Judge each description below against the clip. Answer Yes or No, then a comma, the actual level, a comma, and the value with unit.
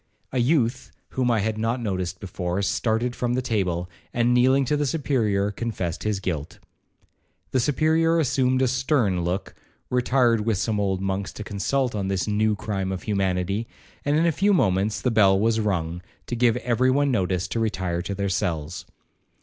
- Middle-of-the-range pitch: No, low, 110 Hz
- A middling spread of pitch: Yes, average, 4.7 semitones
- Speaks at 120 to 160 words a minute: No, average, 180 wpm